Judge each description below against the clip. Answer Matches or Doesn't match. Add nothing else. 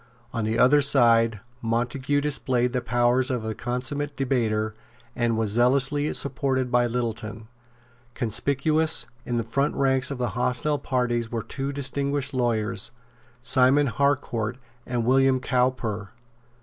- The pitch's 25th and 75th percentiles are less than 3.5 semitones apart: Matches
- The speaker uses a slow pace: Matches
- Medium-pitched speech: Doesn't match